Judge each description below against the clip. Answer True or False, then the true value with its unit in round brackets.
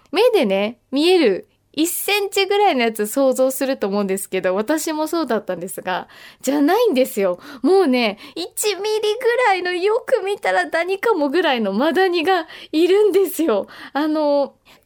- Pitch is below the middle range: False (320 Hz)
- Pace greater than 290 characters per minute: True (320 characters per minute)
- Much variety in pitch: True (7.1 semitones)